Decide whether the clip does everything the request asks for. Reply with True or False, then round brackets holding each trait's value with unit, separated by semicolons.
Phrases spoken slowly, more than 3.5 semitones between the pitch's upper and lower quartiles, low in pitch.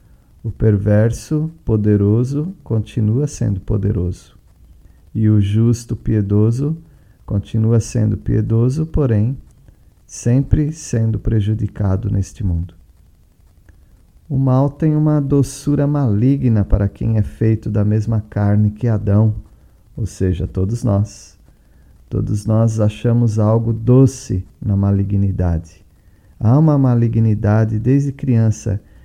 False (105 wpm; 3.2 semitones; 110 Hz)